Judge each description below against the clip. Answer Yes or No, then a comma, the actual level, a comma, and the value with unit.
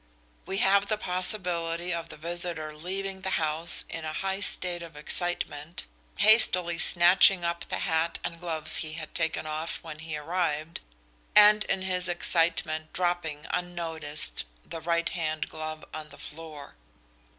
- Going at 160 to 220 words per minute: No, average, 150 wpm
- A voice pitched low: No, medium, 170 Hz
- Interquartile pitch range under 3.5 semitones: Yes, narrow, 2.4 semitones